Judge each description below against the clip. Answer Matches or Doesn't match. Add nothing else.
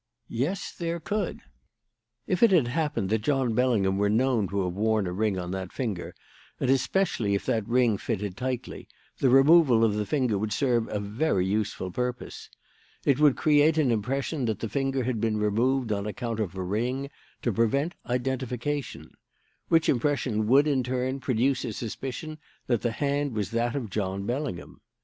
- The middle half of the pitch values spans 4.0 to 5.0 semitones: Matches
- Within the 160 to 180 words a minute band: Matches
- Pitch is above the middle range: Doesn't match